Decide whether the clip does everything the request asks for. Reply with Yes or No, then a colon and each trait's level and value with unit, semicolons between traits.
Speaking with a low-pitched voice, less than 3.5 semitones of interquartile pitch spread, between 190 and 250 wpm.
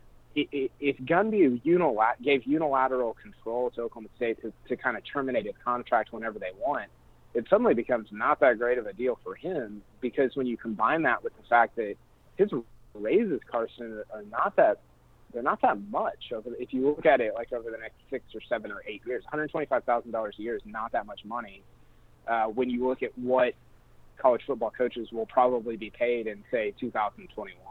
Yes: low, 125 Hz; average, 3.1 semitones; average, 195 wpm